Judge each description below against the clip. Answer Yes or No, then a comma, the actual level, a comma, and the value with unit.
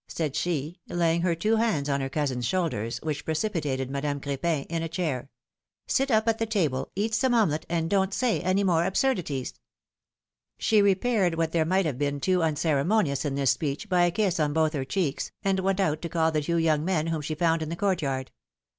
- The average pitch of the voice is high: No, medium, 165 Hz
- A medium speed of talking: No, fast, 220 wpm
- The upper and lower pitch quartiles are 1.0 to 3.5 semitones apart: No, average, 4.5 semitones